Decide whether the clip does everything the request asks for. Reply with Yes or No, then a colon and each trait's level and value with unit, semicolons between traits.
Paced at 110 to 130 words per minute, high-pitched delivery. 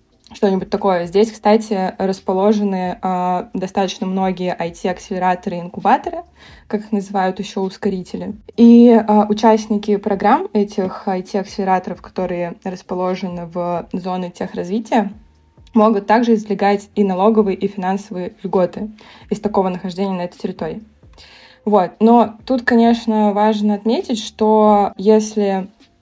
Yes: average, 115 wpm; high, 200 Hz